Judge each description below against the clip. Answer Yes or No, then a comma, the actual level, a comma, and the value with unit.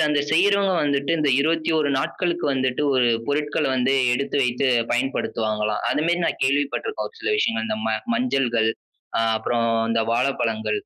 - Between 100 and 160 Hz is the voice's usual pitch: Yes, medium, 140 Hz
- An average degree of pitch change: No, wide, 5.8 semitones